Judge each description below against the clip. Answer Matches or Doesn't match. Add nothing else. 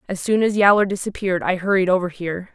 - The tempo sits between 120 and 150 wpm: Doesn't match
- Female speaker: Matches